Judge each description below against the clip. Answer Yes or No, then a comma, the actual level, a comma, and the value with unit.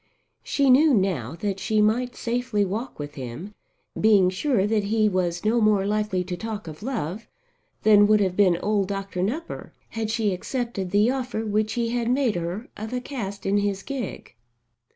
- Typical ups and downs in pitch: Yes, average, 3.4 semitones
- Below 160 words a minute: No, average, 180 wpm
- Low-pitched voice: No, high, 210 Hz